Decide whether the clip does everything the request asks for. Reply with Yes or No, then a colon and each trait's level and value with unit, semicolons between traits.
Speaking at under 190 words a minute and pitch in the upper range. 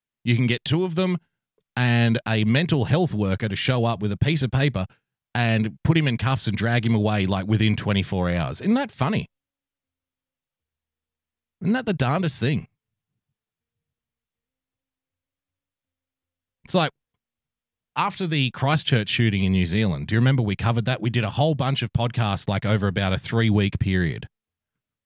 No: average, 165 wpm; low, 115 Hz